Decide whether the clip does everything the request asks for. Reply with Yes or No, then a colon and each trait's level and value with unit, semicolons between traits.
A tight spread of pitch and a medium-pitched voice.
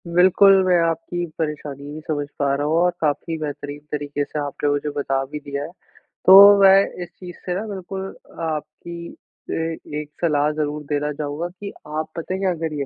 No: average, 3.5 semitones; medium, 155 Hz